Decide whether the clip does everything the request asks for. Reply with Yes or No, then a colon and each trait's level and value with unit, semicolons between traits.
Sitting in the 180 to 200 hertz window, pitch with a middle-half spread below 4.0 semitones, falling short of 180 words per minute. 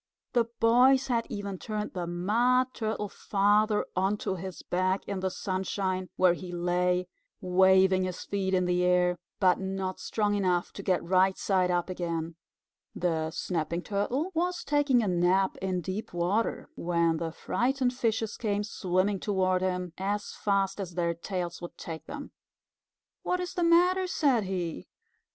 Yes: high, 190 Hz; average, 3.2 semitones; average, 155 wpm